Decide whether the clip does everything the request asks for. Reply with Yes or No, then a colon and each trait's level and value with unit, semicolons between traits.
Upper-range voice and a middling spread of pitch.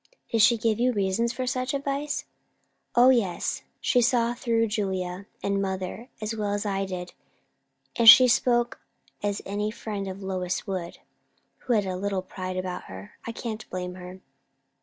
Yes: high, 205 Hz; average, 3.8 semitones